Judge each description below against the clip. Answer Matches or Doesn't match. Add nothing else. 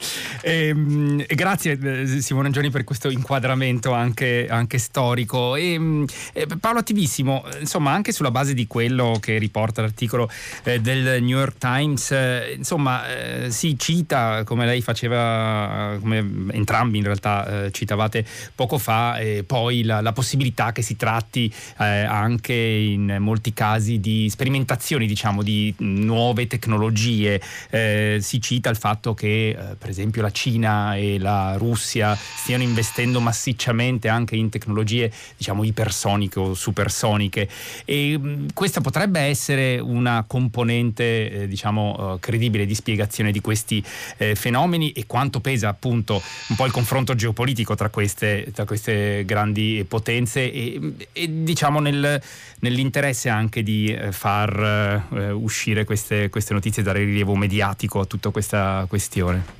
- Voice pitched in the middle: Doesn't match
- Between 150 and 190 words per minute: Doesn't match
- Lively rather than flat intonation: Doesn't match